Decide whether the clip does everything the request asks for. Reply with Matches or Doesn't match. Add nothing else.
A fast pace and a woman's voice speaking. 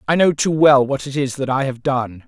Doesn't match